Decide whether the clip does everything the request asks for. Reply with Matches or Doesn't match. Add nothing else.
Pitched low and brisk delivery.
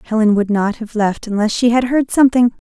Doesn't match